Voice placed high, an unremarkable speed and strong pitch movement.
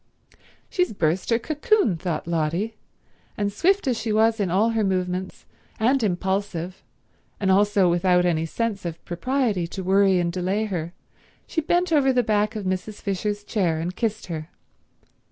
No: high, 200 Hz; average, 160 wpm; average, 4.0 semitones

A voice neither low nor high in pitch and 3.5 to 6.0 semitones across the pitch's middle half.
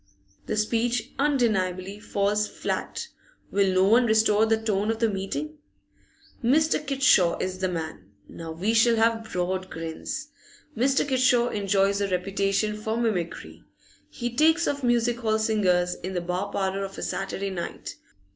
No: high, 210 Hz; average, 4.0 semitones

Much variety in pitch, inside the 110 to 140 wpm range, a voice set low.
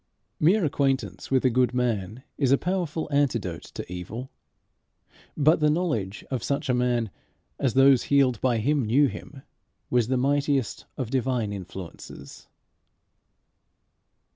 No: average, 3.3 semitones; slow, 135 wpm; low, 130 Hz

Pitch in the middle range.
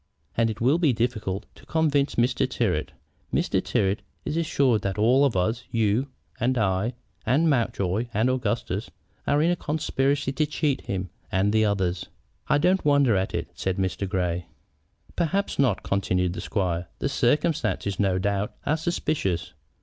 No: low, 115 Hz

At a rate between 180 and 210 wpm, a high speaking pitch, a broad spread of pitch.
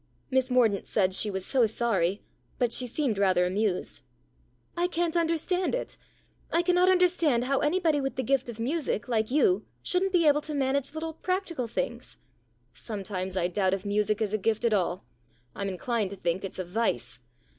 Yes: average, 190 wpm; high, 235 Hz; wide, 7.7 semitones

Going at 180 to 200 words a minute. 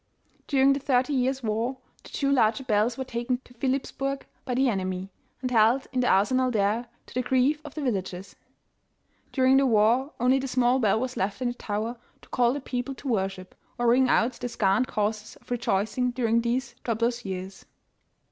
Yes: average, 195 wpm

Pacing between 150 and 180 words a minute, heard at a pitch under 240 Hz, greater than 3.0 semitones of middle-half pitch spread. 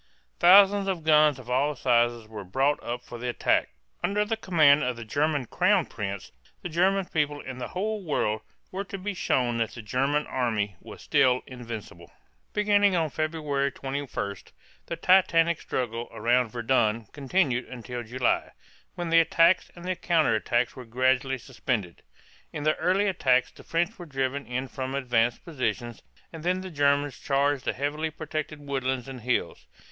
Yes: average, 165 wpm; medium, 140 Hz; average, 5.3 semitones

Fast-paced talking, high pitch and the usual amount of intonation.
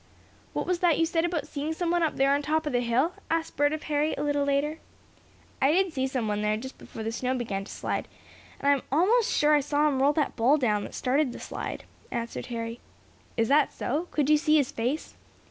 Yes: fast, 230 wpm; very high, 290 Hz; average, 3.8 semitones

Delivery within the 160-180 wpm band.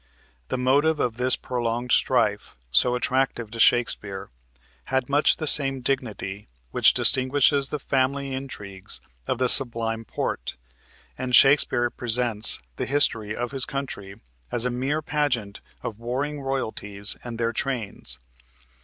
No: slow, 135 wpm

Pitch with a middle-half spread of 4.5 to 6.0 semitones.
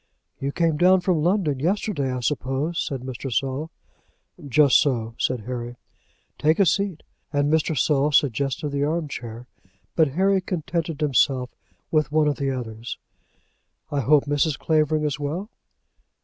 No: average, 3.3 semitones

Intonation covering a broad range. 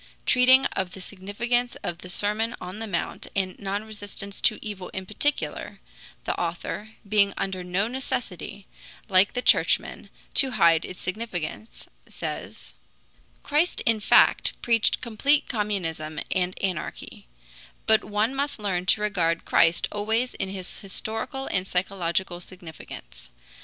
No: average, 3.5 semitones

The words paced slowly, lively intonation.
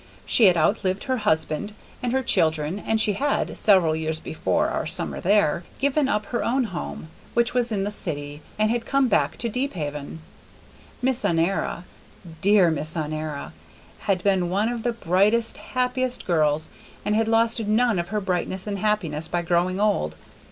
No: average, 170 wpm; wide, 5.9 semitones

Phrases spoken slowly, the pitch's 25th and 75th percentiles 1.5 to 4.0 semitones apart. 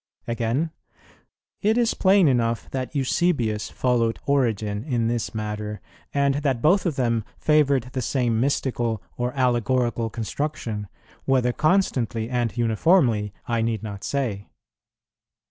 Yes: slow, 130 wpm; average, 3.7 semitones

